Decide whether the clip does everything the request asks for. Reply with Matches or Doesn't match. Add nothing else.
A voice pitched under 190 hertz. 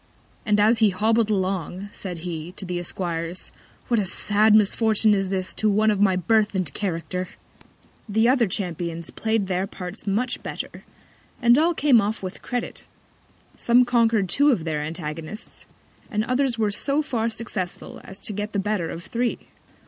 Doesn't match